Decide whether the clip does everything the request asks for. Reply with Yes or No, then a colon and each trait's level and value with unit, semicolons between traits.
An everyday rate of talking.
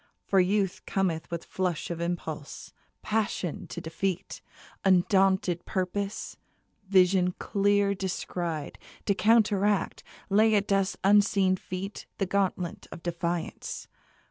No: slow, 110 wpm